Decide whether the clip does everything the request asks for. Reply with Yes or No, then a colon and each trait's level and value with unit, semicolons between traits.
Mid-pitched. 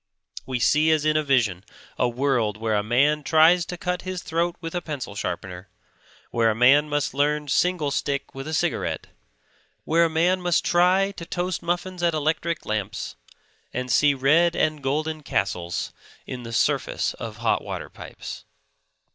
Yes: medium, 150 Hz